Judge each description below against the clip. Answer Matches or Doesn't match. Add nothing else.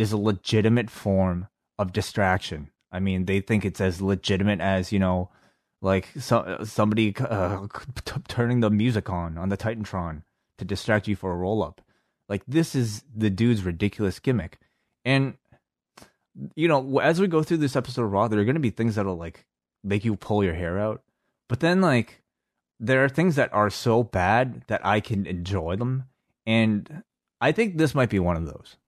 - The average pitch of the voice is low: Matches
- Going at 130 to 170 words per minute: Doesn't match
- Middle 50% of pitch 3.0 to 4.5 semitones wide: Matches